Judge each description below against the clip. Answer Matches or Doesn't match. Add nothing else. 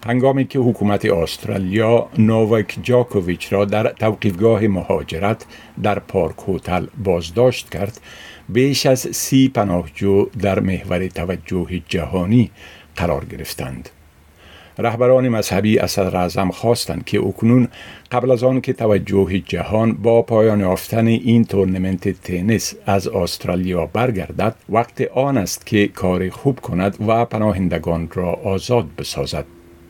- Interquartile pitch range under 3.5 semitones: Doesn't match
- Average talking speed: Matches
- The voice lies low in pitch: Matches